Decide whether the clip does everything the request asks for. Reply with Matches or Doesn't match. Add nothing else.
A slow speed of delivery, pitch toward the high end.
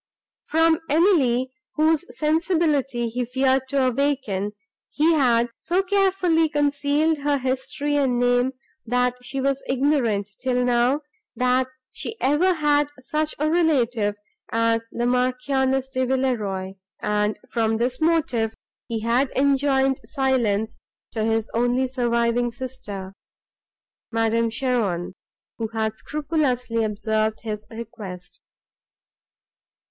Matches